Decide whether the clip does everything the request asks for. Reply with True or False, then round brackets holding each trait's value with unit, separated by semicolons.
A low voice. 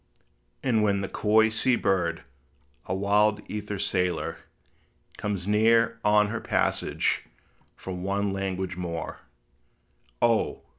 True (100 Hz)